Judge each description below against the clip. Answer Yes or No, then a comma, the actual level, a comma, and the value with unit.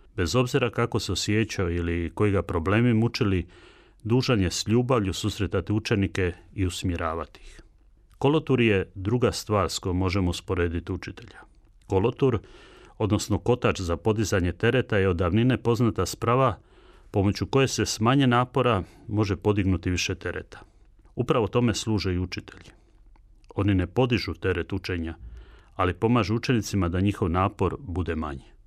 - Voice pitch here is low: Yes, low, 100 Hz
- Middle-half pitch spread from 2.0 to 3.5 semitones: No, average, 4.0 semitones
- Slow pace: No, average, 140 wpm